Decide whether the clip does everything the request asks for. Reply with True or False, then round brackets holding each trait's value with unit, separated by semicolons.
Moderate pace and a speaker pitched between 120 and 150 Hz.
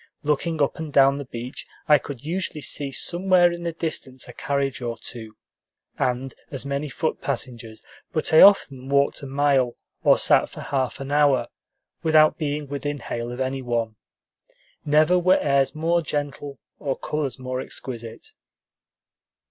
True (155 wpm; 140 Hz)